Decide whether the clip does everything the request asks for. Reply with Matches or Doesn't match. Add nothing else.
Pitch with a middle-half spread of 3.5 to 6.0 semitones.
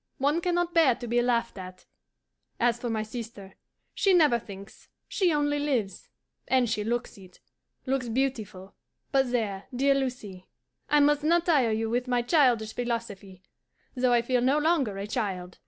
Matches